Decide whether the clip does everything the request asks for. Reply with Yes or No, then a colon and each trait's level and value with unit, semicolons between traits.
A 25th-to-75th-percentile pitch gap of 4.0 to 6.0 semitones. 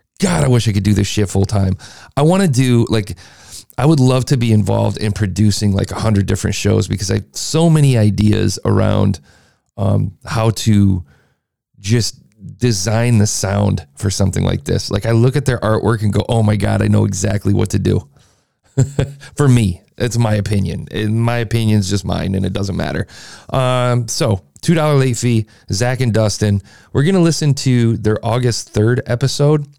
No: average, 3.5 semitones